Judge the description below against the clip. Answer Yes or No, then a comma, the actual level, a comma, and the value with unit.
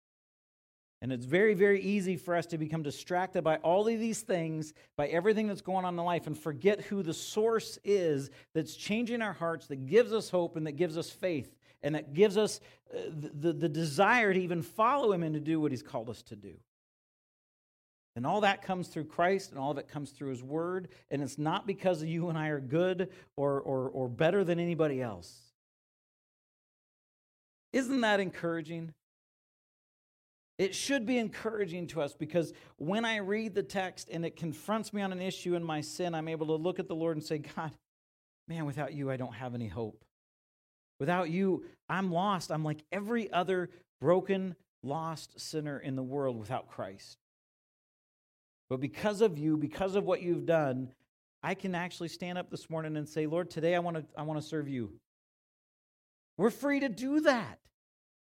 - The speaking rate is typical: Yes, average, 190 wpm